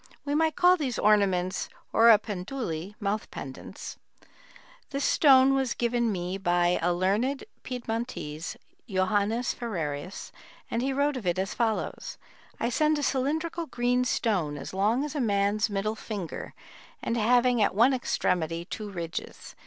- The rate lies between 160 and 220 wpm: No, average, 140 wpm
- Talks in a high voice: Yes, high, 220 Hz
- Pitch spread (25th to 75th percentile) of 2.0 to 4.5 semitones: No, average, 5.3 semitones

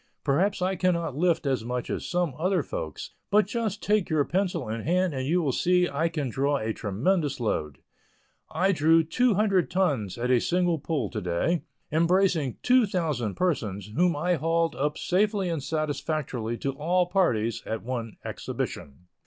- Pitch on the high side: No, medium, 160 Hz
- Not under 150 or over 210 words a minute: Yes, average, 170 wpm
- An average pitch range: No, wide, 6.1 semitones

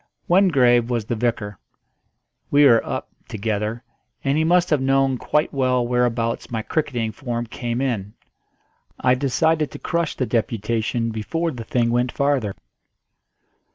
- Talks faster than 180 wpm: No, average, 140 wpm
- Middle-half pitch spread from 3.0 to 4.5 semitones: Yes, average, 3.3 semitones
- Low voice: Yes, low, 125 Hz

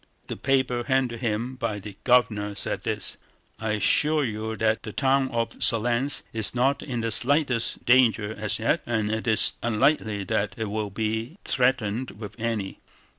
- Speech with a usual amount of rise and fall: Yes, average, 3.0 semitones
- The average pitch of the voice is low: Yes, low, 115 Hz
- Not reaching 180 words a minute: Yes, average, 170 wpm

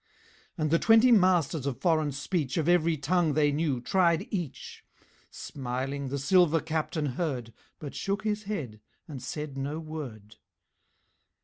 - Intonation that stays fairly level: No, average, 4.2 semitones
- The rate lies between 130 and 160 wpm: Yes, average, 140 wpm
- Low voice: No, medium, 155 Hz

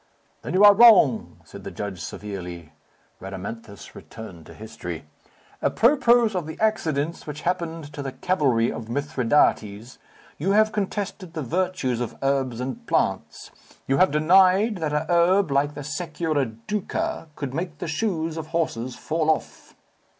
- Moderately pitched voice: Yes, medium, 150 Hz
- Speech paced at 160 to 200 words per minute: No, average, 145 wpm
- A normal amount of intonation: No, wide, 6.9 semitones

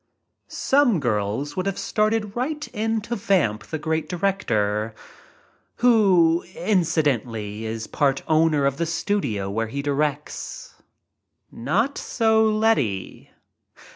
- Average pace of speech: No, slow, 110 wpm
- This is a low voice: No, medium, 160 Hz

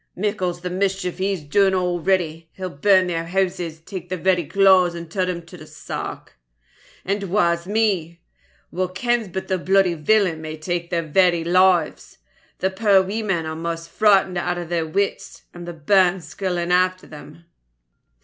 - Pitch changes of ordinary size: No, narrow, 2.2 semitones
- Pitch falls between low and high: Yes, medium, 180 Hz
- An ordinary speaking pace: Yes, average, 165 wpm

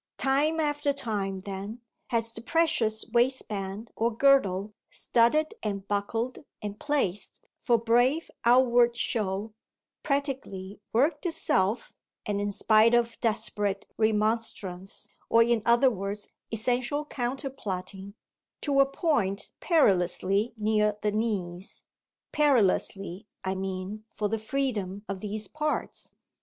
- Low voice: No, high, 220 Hz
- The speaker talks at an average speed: No, slow, 115 wpm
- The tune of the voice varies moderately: Yes, average, 4.2 semitones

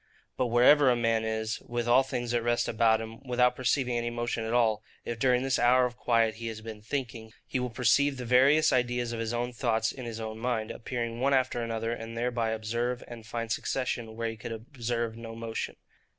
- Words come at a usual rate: No, fast, 210 wpm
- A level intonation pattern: Yes, narrow, 1.6 semitones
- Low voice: Yes, low, 120 Hz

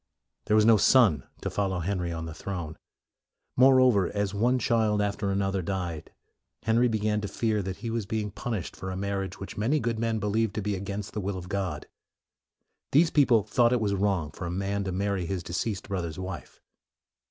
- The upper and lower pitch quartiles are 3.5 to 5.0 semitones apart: No, average, 2.9 semitones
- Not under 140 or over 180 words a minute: No, average, 200 wpm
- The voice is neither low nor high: No, low, 100 Hz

